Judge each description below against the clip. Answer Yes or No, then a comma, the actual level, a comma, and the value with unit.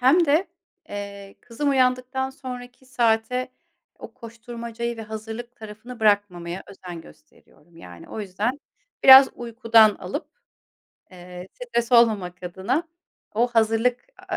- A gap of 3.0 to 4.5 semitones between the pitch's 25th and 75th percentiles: Yes, average, 3.7 semitones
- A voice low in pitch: No, high, 230 Hz